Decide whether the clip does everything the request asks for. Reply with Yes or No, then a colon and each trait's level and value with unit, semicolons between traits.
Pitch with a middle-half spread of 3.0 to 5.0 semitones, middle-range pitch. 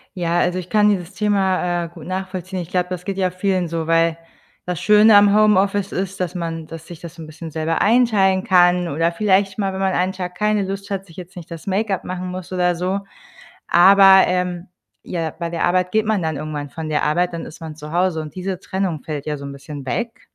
No: narrow, 2.6 semitones; medium, 180 Hz